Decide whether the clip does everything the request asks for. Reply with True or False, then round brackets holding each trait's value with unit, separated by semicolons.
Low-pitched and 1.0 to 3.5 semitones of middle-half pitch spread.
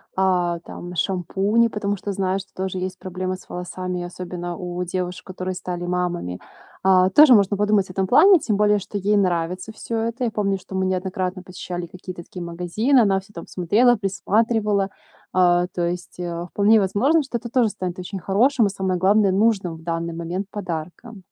False (190 Hz; 2.6 semitones)